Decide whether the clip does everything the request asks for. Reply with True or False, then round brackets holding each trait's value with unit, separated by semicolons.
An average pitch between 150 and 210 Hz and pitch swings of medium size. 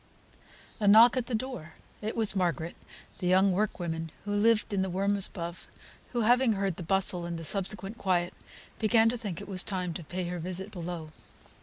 True (190 Hz; 3.5 semitones)